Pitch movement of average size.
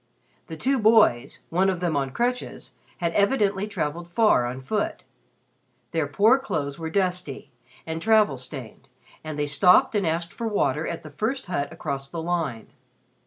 No: wide, 6.2 semitones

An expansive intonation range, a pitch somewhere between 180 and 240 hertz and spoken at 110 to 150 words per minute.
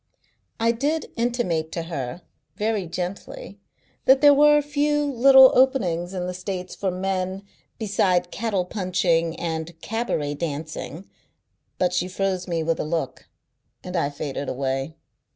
Yes: wide, 5.7 semitones; medium, 185 Hz; average, 140 wpm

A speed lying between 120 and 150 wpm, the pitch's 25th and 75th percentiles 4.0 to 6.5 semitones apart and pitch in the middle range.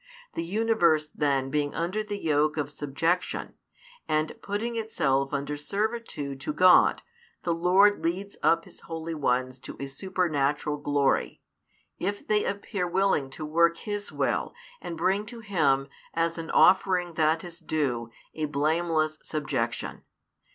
Yes: average, 140 wpm; average, 4.3 semitones; medium, 165 Hz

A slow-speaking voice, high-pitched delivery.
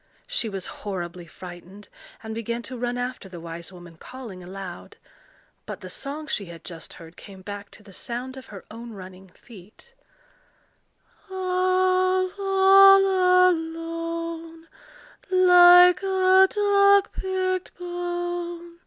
Yes: slow, 125 wpm; very high, 325 Hz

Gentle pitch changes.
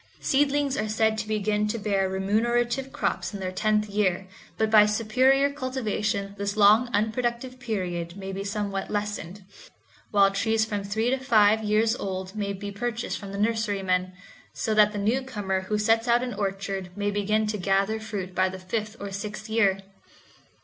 Yes: narrow, 2.2 semitones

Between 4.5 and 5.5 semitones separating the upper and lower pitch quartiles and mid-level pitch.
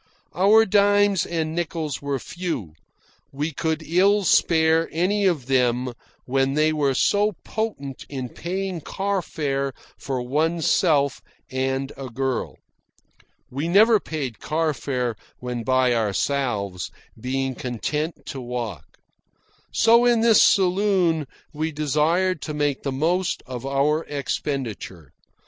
Yes: average, 5.1 semitones; medium, 150 Hz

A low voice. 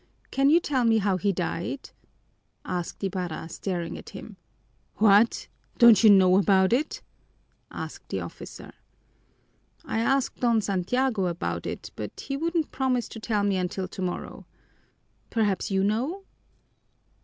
No: high, 205 Hz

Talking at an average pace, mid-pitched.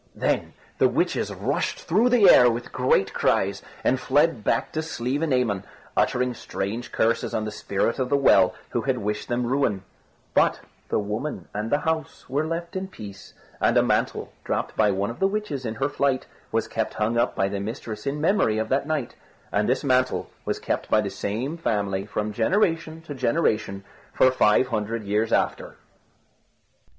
No: average, 180 wpm; low, 125 Hz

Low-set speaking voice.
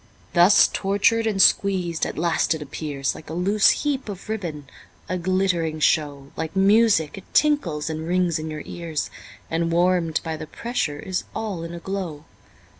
No: medium, 170 Hz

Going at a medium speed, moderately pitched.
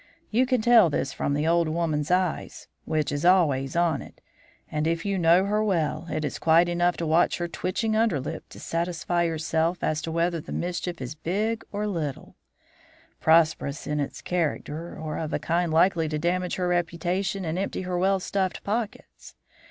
Yes: average, 185 wpm; medium, 170 Hz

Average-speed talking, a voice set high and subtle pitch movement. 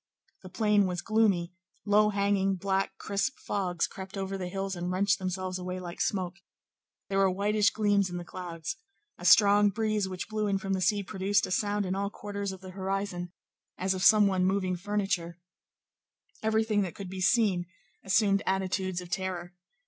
Yes: average, 180 wpm; high, 195 Hz; narrow, 1.8 semitones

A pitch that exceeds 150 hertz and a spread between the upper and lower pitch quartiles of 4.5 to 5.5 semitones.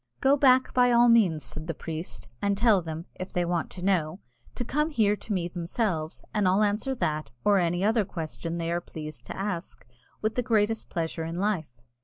Yes: high, 190 Hz; average, 4.8 semitones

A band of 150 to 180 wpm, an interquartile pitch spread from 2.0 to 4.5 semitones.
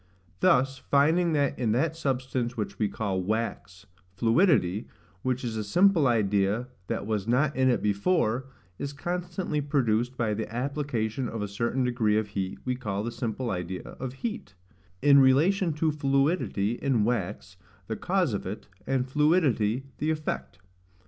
No: average, 155 wpm; average, 5.0 semitones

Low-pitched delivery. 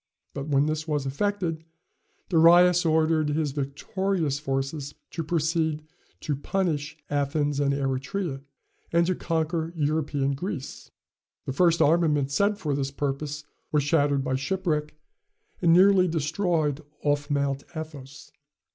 No: medium, 150 Hz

